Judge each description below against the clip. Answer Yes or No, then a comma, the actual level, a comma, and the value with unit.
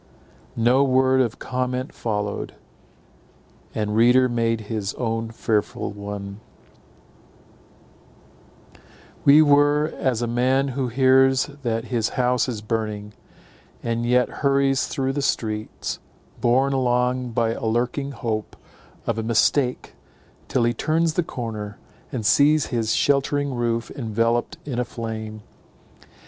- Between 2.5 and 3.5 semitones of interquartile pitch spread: Yes, average, 2.9 semitones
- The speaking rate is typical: No, slow, 120 wpm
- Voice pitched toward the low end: Yes, low, 120 Hz